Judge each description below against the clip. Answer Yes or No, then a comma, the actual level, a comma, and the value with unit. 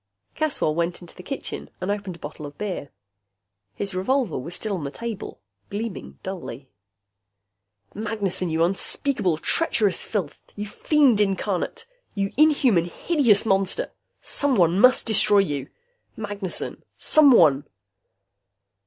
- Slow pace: Yes, slow, 120 wpm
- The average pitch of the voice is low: No, high, 200 Hz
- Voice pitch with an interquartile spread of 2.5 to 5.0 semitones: Yes, average, 4.6 semitones